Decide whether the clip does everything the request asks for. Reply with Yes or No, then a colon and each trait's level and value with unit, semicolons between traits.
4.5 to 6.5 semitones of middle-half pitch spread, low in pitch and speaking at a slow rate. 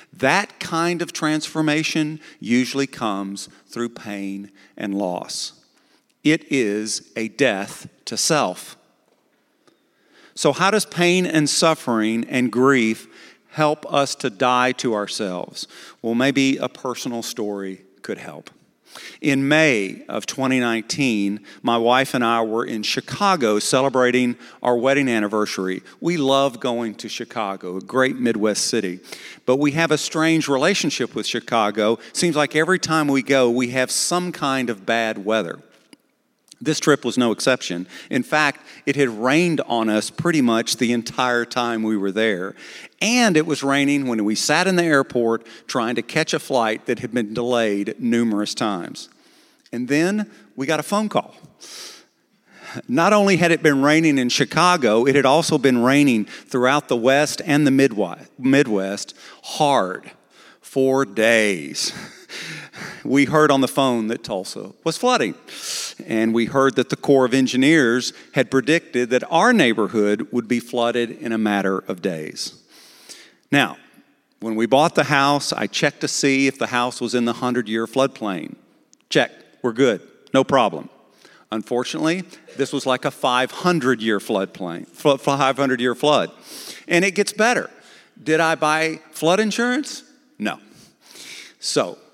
No: average, 5.0 semitones; low, 130 Hz; average, 145 wpm